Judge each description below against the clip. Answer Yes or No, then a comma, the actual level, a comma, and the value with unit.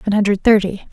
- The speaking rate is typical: Yes, average, 195 wpm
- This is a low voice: No, high, 200 Hz